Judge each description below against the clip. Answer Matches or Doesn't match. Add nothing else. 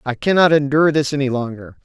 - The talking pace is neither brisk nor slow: Matches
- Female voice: Doesn't match